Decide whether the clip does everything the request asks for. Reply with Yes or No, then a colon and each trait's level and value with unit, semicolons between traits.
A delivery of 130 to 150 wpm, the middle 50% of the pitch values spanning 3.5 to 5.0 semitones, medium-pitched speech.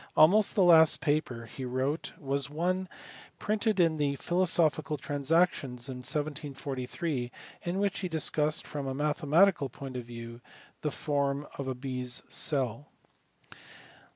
Yes: average, 140 wpm; average, 3.9 semitones; medium, 145 Hz